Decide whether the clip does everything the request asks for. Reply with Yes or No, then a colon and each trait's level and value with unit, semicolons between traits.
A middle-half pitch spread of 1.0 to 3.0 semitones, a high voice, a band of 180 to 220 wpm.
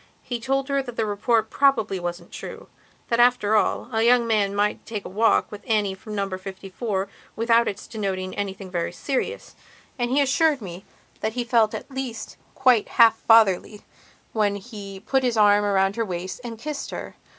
No: average, 3.5 semitones; high, 220 Hz; average, 185 wpm